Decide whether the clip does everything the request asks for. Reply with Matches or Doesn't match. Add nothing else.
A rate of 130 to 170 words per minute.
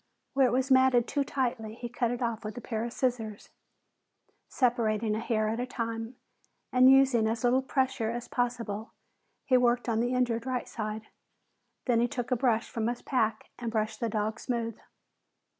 Doesn't match